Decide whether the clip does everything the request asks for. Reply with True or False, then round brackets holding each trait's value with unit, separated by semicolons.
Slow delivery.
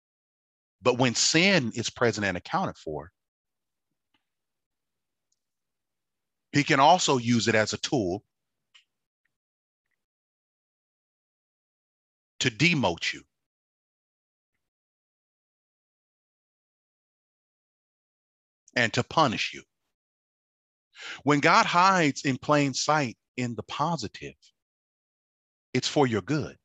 True (80 wpm)